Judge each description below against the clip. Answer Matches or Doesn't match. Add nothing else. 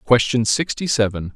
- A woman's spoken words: Doesn't match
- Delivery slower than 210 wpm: Matches